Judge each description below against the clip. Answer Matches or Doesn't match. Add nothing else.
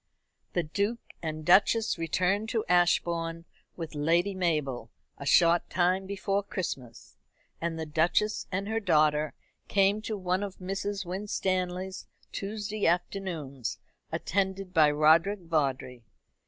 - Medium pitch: Matches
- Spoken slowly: Matches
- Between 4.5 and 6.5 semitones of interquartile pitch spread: Doesn't match